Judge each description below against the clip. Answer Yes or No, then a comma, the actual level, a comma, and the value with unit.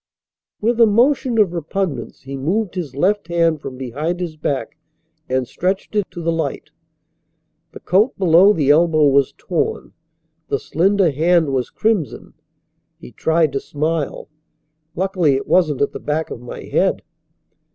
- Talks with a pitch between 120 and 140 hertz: No, medium, 165 Hz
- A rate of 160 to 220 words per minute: No, average, 150 wpm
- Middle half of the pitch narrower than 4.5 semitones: No, average, 4.9 semitones